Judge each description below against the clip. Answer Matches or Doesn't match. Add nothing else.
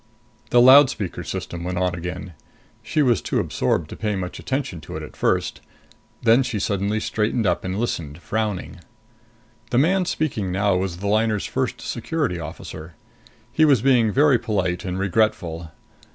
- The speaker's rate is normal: Matches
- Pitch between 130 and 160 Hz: Doesn't match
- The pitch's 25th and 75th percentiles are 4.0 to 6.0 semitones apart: Matches